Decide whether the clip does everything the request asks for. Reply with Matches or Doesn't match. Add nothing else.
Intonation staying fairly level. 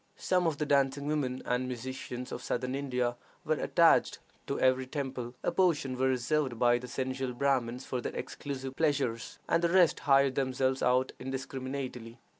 Matches